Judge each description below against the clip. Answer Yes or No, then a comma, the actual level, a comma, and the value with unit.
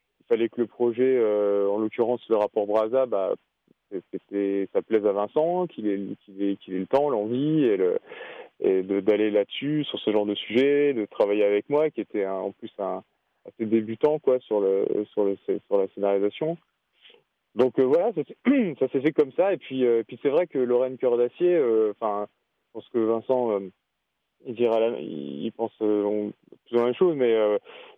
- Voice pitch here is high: No, low, 115 Hz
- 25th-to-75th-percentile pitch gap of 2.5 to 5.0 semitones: No, wide, 5.5 semitones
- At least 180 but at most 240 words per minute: Yes, average, 205 wpm